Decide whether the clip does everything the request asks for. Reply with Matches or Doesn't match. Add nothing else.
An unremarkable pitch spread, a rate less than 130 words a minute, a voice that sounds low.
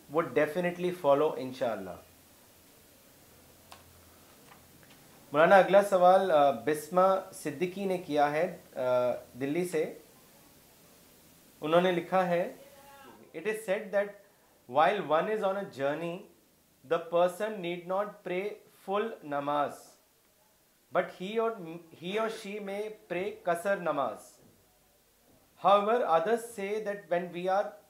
Doesn't match